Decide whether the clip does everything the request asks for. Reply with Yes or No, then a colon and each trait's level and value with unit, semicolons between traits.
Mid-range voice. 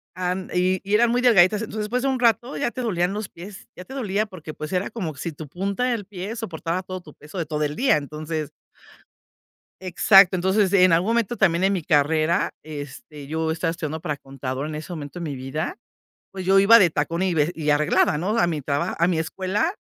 Yes: medium, 180 Hz